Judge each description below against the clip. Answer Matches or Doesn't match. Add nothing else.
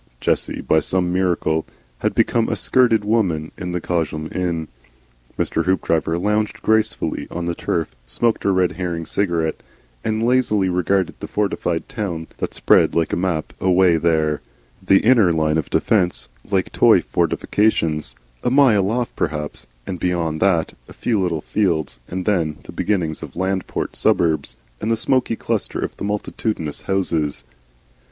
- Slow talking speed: Doesn't match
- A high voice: Doesn't match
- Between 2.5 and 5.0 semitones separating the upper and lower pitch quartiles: Matches